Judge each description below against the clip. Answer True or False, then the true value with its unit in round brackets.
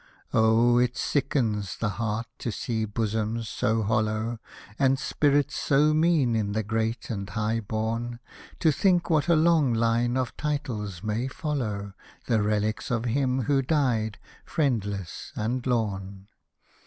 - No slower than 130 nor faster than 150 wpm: True (145 wpm)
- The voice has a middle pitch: False (115 Hz)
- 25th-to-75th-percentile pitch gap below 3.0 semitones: False (3.8 semitones)